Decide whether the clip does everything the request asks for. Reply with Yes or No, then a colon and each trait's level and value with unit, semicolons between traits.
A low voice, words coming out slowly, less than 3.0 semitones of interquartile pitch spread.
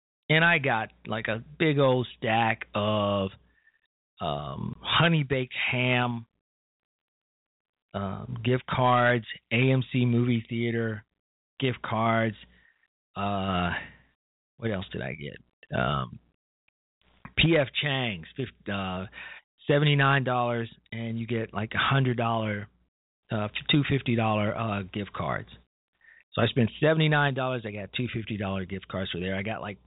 No: low, 115 Hz; slow, 110 wpm; average, 4.2 semitones